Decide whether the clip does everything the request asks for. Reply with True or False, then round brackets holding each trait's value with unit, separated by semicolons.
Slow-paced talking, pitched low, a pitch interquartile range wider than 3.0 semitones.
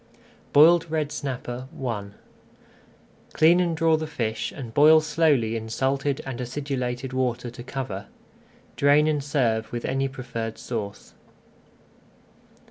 True (125 wpm; 130 Hz; 4.0 semitones)